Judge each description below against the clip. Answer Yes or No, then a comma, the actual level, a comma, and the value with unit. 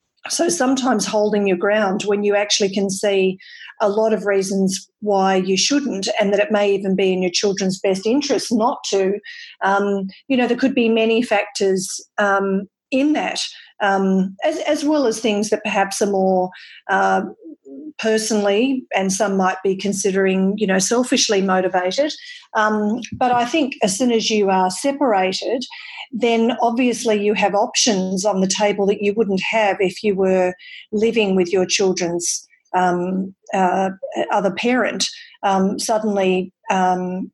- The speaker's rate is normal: Yes, average, 160 wpm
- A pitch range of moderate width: Yes, average, 3.5 semitones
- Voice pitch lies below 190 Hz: No, high, 205 Hz